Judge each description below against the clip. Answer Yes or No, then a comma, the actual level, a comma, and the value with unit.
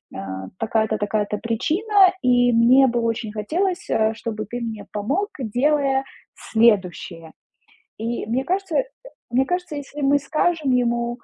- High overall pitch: Yes, high, 240 Hz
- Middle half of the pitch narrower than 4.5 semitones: No, average, 4.9 semitones